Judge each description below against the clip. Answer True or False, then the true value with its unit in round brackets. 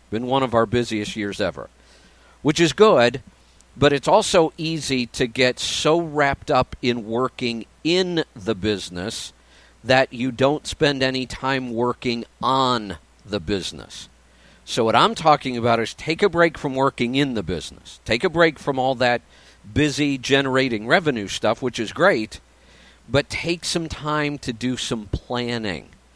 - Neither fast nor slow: True (160 wpm)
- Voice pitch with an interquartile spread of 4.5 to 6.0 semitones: True (5.2 semitones)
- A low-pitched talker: True (125 Hz)